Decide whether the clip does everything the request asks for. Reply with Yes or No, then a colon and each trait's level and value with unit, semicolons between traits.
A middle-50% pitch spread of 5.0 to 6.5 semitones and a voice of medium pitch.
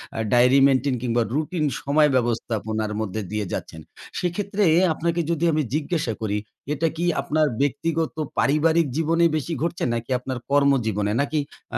Yes: wide, 5.5 semitones; medium, 145 Hz